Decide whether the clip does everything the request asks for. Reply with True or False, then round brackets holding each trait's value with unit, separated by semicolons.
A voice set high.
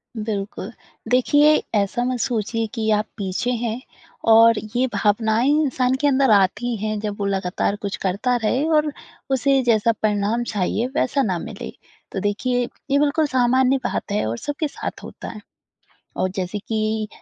True (225 Hz)